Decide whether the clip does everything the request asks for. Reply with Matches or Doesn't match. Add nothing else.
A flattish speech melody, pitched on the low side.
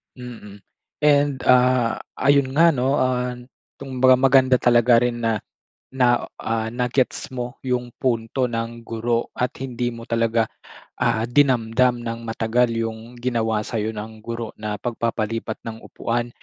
Matches